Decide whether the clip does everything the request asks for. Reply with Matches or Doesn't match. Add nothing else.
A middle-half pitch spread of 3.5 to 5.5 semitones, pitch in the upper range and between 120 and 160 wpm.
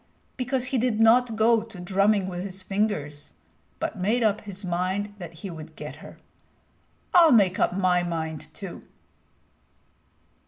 Matches